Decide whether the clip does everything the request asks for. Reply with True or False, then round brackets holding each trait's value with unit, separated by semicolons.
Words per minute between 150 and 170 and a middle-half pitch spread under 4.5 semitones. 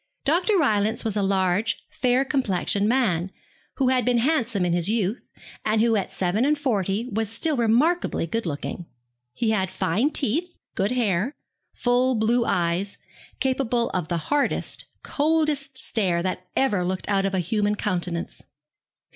False (155 wpm; 5.4 semitones)